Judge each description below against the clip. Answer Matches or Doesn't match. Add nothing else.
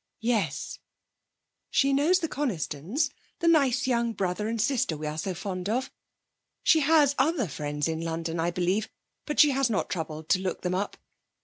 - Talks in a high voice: Matches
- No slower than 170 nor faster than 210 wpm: Matches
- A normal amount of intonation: Doesn't match